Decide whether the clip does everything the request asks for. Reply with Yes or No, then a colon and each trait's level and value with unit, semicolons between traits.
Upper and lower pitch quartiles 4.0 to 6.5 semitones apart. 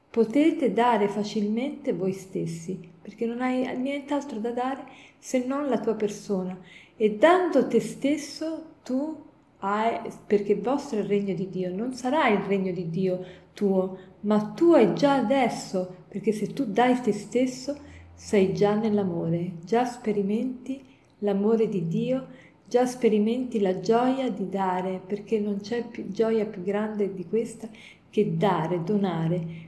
Yes: average, 4.7 semitones